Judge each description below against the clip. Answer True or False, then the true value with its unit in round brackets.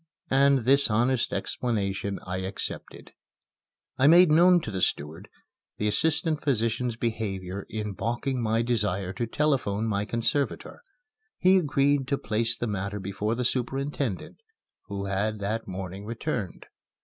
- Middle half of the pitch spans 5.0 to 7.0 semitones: True (5.3 semitones)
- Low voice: True (115 Hz)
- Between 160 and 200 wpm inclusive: False (135 wpm)